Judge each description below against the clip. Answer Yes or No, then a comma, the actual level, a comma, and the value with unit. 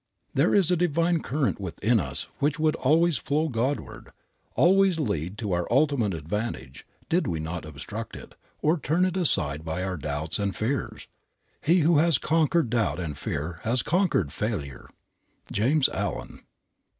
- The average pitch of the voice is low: Yes, low, 120 Hz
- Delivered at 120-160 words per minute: Yes, average, 155 wpm